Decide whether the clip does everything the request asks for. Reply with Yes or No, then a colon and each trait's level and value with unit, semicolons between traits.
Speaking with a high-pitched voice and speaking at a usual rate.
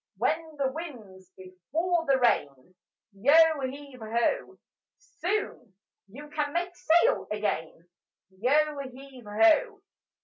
No: very high, 275 Hz; slow, 105 wpm